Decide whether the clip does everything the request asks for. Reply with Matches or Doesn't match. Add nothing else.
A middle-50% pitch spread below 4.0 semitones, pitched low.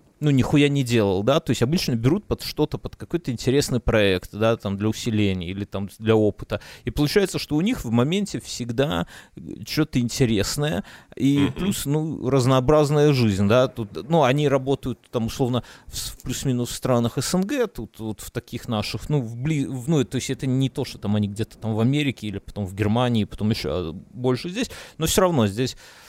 Doesn't match